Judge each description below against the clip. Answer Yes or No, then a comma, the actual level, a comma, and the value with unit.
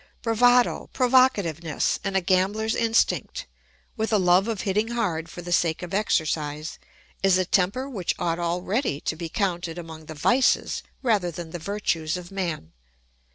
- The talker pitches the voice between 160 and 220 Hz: Yes, medium, 185 Hz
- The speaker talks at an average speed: Yes, average, 155 wpm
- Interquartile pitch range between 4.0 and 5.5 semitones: Yes, average, 4.7 semitones